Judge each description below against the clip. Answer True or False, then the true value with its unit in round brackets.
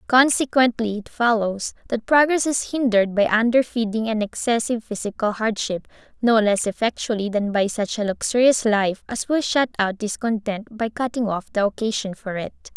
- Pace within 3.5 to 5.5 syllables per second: True (5.1 syllables/s)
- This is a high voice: True (225 Hz)